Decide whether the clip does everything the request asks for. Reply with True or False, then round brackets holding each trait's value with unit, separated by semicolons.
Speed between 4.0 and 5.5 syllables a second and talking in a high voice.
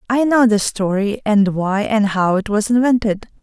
True (4.5 syllables/s; 215 Hz)